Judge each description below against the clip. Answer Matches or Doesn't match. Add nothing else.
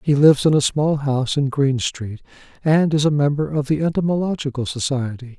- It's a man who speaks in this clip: Matches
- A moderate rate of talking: Matches